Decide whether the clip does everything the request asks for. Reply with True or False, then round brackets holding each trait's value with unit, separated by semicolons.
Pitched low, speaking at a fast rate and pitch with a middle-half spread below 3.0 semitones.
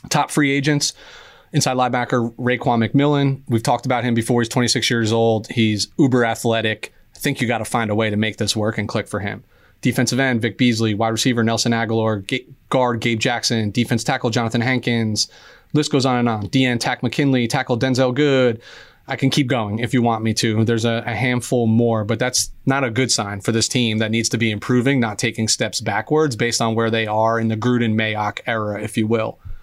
True (120 Hz; 215 wpm; 2.5 semitones)